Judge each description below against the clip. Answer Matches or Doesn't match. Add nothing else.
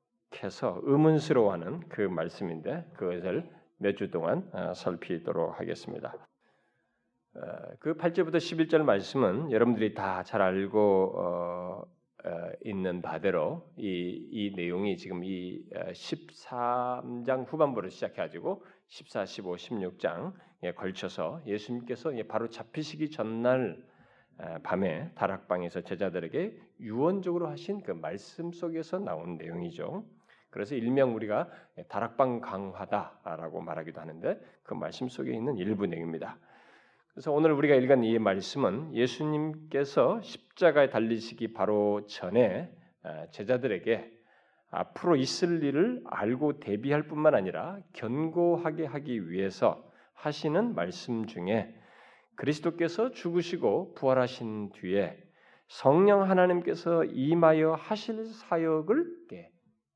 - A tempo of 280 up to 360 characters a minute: Doesn't match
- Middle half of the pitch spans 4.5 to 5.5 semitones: Doesn't match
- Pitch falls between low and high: Doesn't match